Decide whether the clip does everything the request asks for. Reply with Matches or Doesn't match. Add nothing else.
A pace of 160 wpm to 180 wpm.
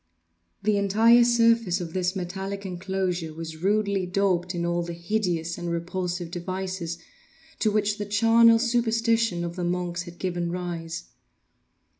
Doesn't match